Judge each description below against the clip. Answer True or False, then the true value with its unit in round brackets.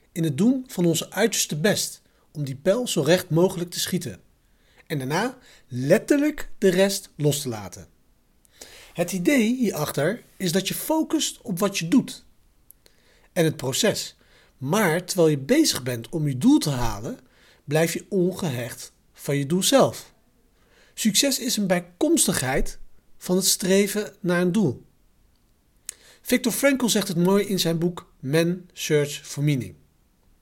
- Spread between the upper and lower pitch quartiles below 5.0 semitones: False (5.5 semitones)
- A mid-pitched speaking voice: True (180 Hz)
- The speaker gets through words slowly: False (150 wpm)